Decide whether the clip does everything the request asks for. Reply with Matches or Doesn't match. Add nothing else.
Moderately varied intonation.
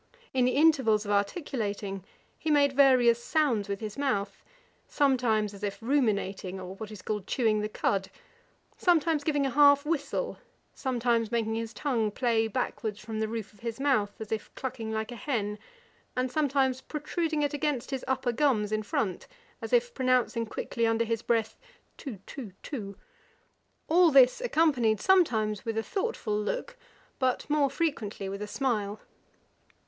Matches